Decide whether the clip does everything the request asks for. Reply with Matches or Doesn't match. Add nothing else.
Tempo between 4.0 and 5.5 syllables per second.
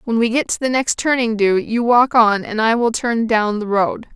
Matches